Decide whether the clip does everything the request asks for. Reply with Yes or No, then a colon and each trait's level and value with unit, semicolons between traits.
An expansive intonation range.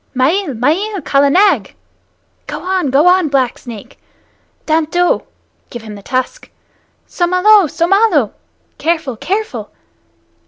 Yes: wide, 6.3 semitones